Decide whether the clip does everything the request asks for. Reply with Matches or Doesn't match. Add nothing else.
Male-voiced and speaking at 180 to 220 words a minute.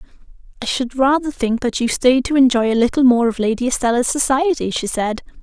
Doesn't match